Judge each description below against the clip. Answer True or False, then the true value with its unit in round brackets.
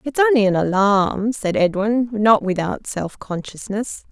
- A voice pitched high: True (210 Hz)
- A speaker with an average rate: True (145 wpm)